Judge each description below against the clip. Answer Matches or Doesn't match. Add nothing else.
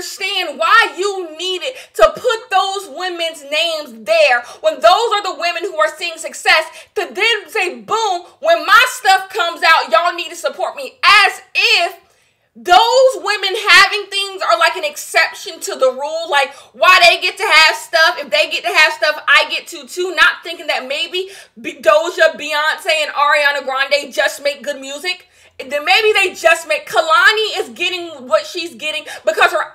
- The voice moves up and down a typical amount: Matches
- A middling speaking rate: Matches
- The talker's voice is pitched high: Matches